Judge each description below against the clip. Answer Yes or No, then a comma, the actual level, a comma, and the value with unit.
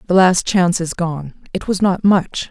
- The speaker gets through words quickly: Yes, fast, 215 wpm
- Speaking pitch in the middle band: Yes, medium, 180 Hz